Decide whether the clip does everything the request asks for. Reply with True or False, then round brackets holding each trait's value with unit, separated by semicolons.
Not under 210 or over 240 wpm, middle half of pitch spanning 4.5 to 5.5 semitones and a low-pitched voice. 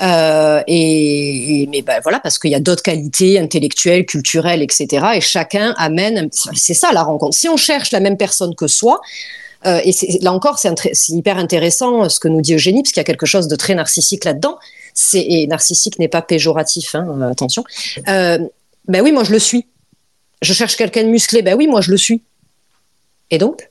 False (215 wpm; 5.2 semitones; 180 Hz)